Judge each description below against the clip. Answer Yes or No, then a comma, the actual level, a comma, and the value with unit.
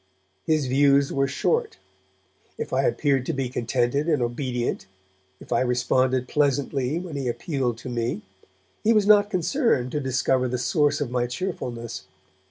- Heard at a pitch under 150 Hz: Yes, low, 135 Hz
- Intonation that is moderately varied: Yes, average, 3.9 semitones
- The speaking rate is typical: Yes, average, 155 wpm